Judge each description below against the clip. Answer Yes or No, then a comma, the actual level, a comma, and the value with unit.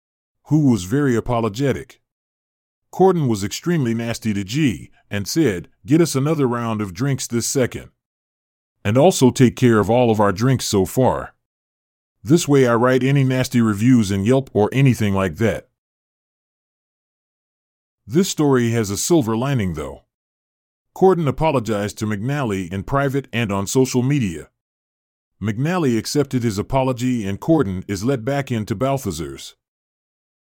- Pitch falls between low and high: No, low, 120 Hz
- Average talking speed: Yes, average, 145 wpm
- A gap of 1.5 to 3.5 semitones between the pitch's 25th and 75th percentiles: No, average, 5.1 semitones